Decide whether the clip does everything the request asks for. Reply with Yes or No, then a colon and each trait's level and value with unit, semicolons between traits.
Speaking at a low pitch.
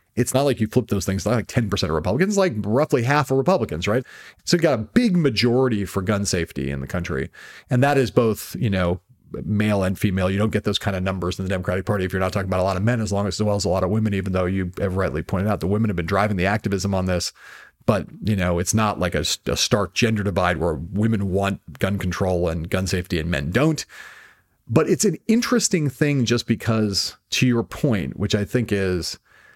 Yes: low, 100 Hz